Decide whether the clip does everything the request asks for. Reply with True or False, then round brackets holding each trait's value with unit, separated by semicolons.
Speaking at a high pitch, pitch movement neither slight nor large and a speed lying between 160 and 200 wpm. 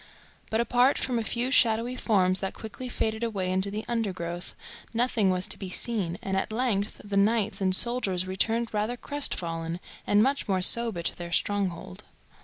True (210 Hz; 4.0 semitones; 175 wpm)